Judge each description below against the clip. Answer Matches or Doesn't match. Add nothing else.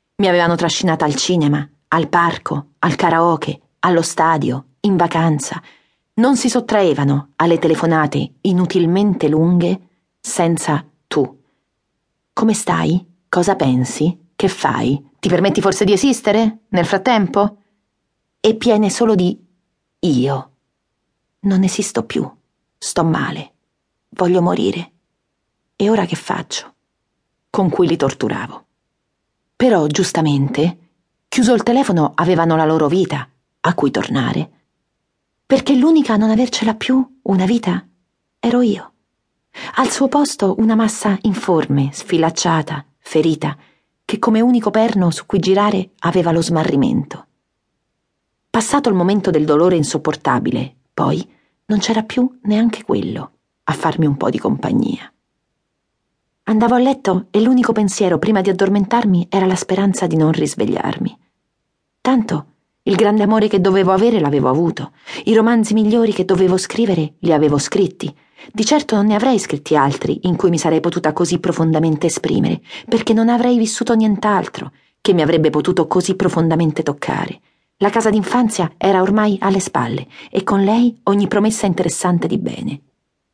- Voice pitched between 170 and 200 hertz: Matches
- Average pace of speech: Matches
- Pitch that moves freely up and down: Doesn't match